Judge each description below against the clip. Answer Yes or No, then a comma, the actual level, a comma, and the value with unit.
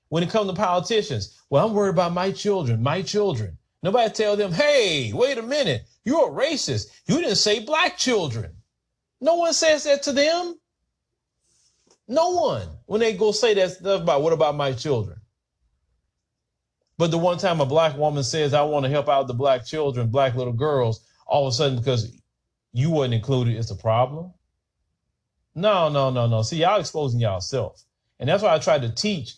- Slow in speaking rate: No, average, 190 wpm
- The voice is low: No, medium, 150 Hz